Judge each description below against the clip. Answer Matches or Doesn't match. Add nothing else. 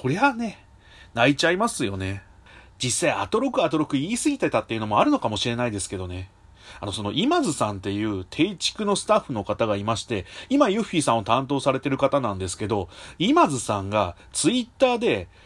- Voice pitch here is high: Doesn't match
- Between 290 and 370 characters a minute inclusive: Doesn't match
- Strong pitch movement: Matches